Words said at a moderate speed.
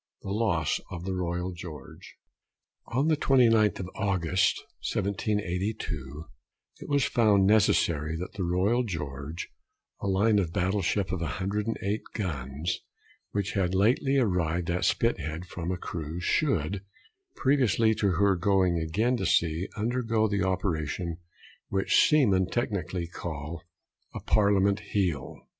No: slow, 130 wpm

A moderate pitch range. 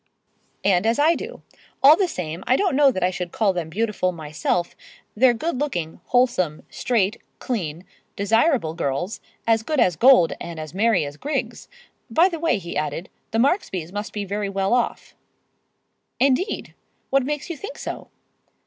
No: wide, 7.2 semitones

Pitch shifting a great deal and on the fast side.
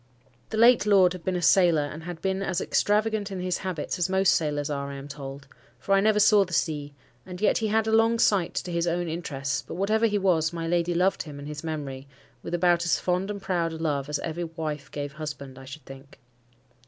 No: average, 4.5 semitones; fast, 230 wpm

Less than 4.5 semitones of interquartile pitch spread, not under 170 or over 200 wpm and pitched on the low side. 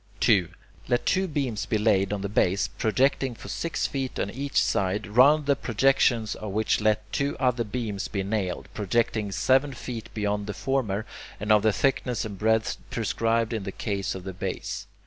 Yes: average, 3.8 semitones; average, 185 wpm; low, 110 Hz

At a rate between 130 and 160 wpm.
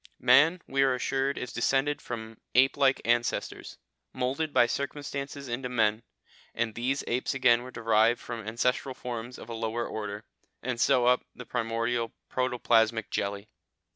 Yes: average, 155 wpm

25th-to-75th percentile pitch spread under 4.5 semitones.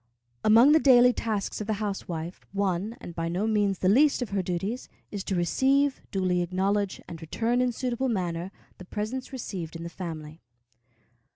No: average, 5.2 semitones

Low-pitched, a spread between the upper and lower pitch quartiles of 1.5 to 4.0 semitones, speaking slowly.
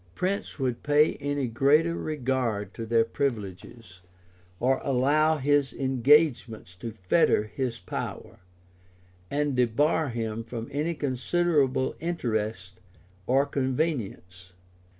No: low, 130 Hz; average, 4.5 semitones; slow, 105 wpm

